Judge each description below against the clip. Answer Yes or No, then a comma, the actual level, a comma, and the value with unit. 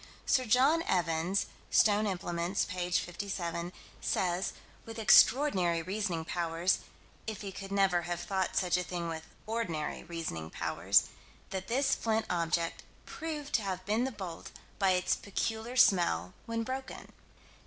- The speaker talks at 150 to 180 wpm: No, average, 140 wpm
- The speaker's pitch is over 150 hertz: Yes, medium, 185 Hz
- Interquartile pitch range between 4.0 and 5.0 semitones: Yes, average, 4.3 semitones